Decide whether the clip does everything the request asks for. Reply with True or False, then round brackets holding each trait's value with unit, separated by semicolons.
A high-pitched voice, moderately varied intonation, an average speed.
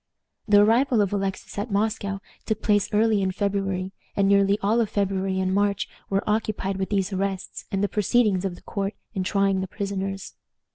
False (200 Hz; 1.2 semitones; 185 wpm)